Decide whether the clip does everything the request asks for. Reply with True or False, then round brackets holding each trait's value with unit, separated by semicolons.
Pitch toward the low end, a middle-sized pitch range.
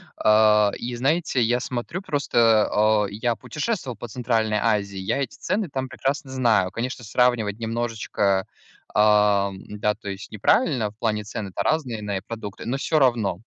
True (115 Hz; 3.3 semitones)